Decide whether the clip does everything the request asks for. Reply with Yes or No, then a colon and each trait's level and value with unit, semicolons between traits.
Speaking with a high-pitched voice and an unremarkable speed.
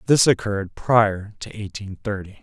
No: low, 105 Hz; average, 150 wpm